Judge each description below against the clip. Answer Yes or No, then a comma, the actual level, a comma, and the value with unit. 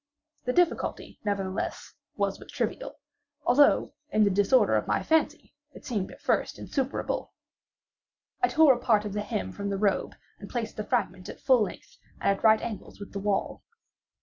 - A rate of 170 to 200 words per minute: Yes, average, 175 wpm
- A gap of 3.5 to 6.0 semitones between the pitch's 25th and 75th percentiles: Yes, average, 4.0 semitones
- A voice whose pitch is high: Yes, high, 210 Hz